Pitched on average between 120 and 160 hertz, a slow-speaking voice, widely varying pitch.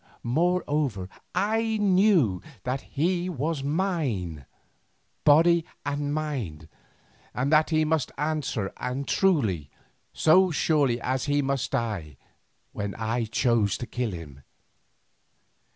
Yes: medium, 140 Hz; slow, 110 wpm; wide, 6.2 semitones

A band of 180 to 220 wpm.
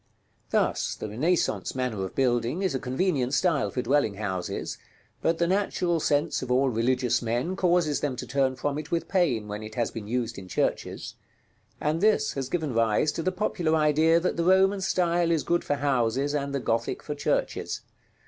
Yes: average, 190 wpm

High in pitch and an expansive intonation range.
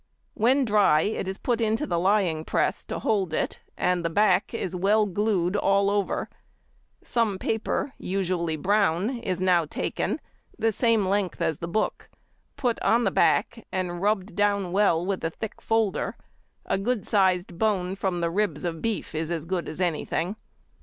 No: high, 195 Hz; average, 3.4 semitones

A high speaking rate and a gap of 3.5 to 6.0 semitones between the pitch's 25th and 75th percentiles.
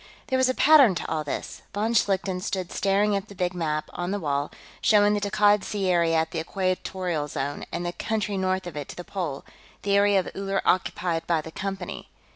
No: fast, 215 wpm; average, 3.1 semitones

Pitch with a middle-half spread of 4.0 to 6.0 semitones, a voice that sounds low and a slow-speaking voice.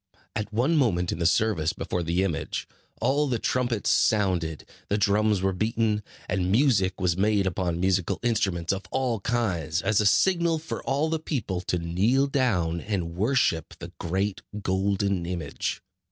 No: average, 4.8 semitones; low, 100 Hz; average, 160 wpm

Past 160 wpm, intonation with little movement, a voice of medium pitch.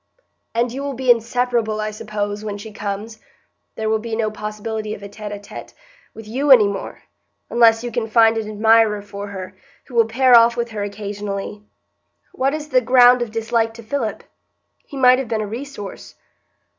No: average, 190 wpm; narrow, 2.3 semitones; high, 225 Hz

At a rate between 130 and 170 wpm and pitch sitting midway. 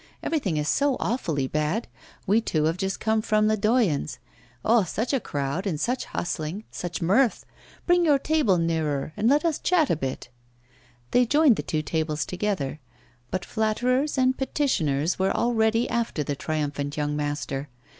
No: average, 160 wpm; high, 195 Hz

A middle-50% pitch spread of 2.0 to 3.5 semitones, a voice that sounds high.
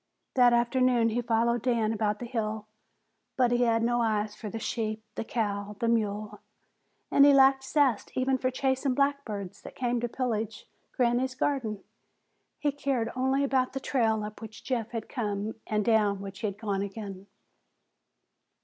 Yes: average, 3.2 semitones; high, 230 Hz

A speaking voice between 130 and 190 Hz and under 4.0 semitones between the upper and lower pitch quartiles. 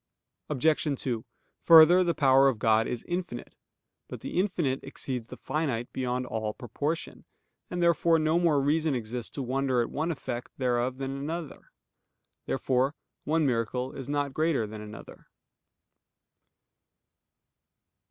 No: low, 135 Hz; average, 4.3 semitones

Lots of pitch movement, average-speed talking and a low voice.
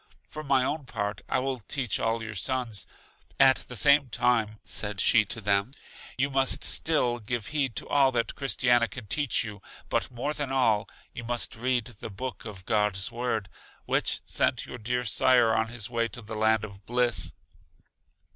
No: average, 3.2 semitones; average, 180 wpm; low, 120 Hz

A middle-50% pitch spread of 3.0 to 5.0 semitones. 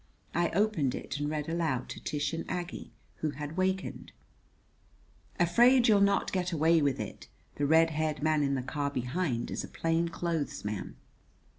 Yes: average, 3.4 semitones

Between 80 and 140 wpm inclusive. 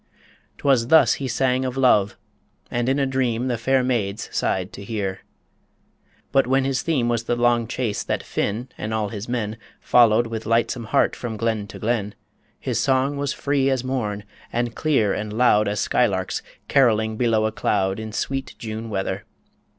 No: average, 175 wpm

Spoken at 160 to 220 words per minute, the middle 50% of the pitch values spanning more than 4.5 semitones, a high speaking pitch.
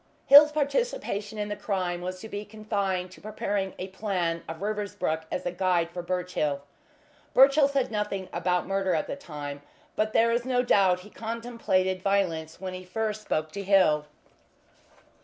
No: average, 165 wpm; average, 3.2 semitones; high, 195 Hz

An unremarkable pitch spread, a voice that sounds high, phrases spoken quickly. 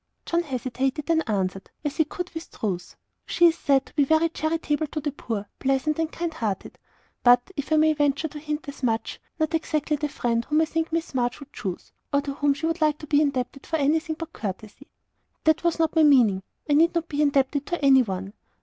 Yes: average, 3.5 semitones; very high, 295 Hz; fast, 220 wpm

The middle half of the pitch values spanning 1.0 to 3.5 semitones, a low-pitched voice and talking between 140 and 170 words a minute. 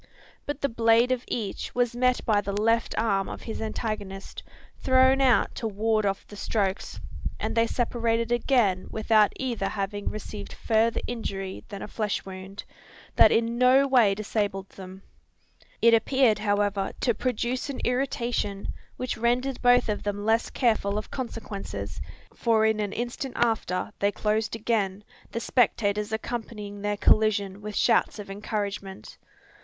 No: average, 2.8 semitones; high, 220 Hz; average, 150 wpm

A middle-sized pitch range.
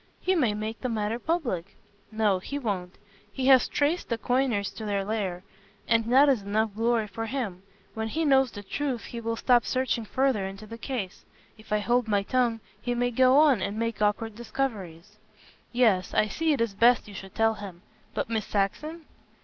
Yes: average, 3.7 semitones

